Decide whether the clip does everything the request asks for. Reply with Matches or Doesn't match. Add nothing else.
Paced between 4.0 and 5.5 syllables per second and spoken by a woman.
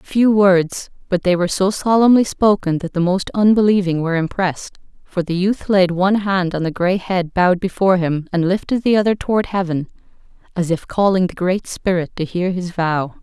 Matches